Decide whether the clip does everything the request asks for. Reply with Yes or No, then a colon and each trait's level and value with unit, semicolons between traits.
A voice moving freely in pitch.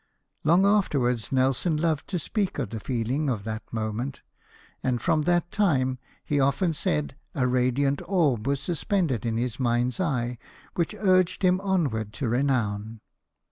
Yes: wide, 6.0 semitones